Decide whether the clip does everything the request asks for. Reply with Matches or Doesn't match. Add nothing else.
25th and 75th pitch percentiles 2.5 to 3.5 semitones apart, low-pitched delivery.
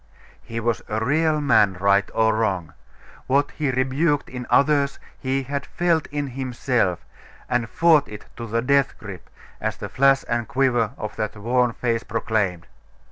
Doesn't match